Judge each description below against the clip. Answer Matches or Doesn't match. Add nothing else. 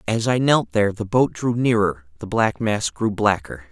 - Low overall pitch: Matches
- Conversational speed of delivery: Doesn't match